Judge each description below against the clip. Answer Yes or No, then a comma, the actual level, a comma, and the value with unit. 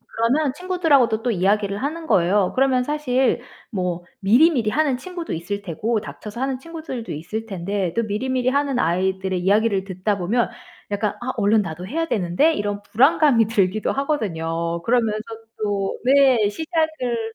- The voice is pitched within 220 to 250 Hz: Yes, high, 225 Hz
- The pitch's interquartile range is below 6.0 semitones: Yes, wide, 5.4 semitones